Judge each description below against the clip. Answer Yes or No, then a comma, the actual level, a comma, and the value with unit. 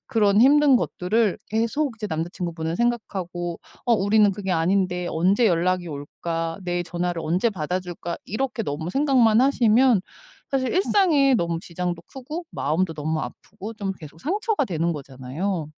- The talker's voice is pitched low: No, medium, 185 Hz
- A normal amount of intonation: No, wide, 5.8 semitones